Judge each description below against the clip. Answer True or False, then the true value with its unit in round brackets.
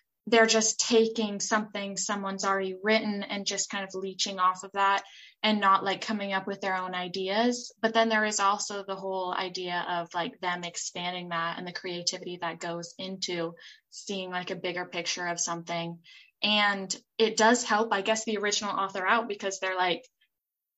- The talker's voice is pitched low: False (195 Hz)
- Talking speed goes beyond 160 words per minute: True (180 wpm)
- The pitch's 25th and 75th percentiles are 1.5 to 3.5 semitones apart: True (2.8 semitones)